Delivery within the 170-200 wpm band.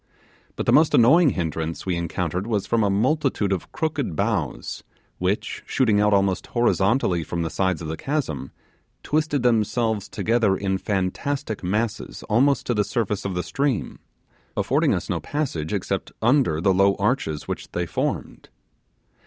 No: average, 155 wpm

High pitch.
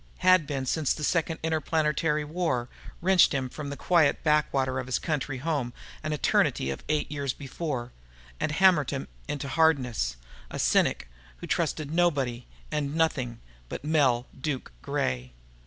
No: medium, 145 Hz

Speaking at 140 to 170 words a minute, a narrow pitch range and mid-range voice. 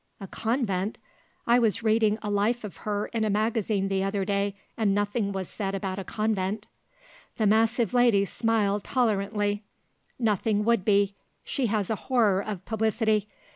No: average, 160 wpm; narrow, 2.0 semitones; high, 210 Hz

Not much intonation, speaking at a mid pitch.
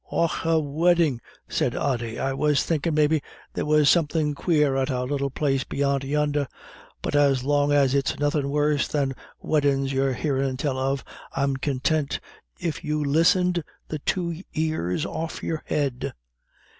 Yes: narrow, 2.2 semitones; medium, 145 Hz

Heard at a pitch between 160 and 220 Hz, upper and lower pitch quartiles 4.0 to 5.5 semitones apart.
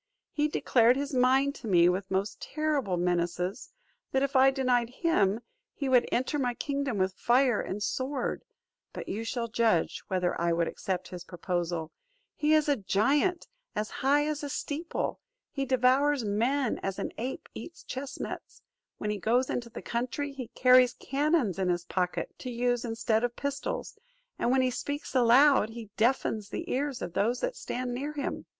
No: high, 245 Hz; average, 5.1 semitones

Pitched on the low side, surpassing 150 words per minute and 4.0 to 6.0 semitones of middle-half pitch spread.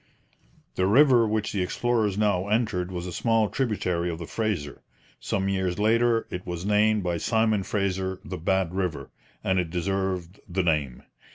No: very low, 95 Hz; average, 165 wpm; average, 3.3 semitones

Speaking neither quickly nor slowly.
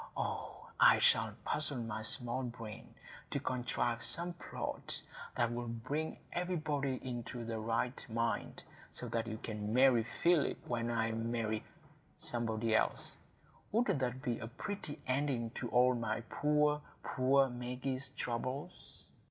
No: slow, 130 wpm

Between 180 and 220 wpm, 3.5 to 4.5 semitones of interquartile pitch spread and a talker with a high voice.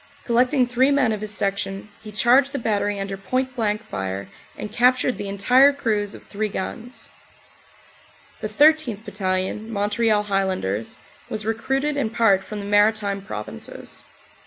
No: average, 145 wpm; average, 3.8 semitones; high, 215 Hz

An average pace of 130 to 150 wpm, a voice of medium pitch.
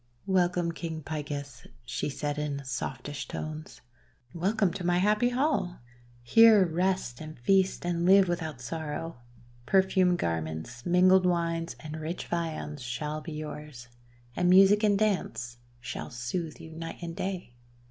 Yes: average, 140 wpm; medium, 165 Hz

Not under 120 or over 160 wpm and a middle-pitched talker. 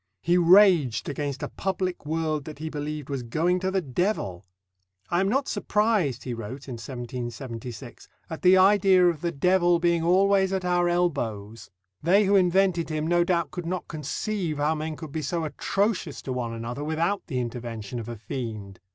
No: average, 180 wpm; medium, 160 Hz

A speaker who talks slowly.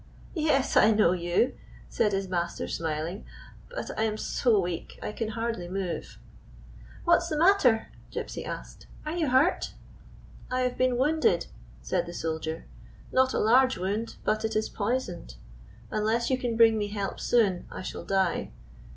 No: average, 175 wpm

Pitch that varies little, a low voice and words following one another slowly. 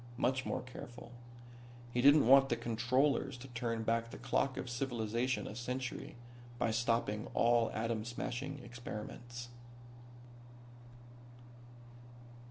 Yes: narrow, 1.9 semitones; low, 120 Hz; slow, 110 wpm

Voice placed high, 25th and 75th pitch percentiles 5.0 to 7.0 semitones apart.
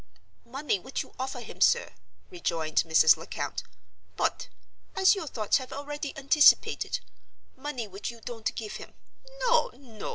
Yes: very high, 260 Hz; average, 5.3 semitones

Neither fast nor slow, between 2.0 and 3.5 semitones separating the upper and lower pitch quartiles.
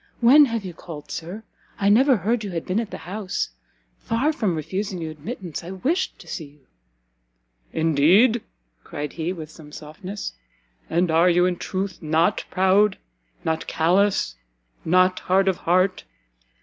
No: average, 155 wpm; average, 4.1 semitones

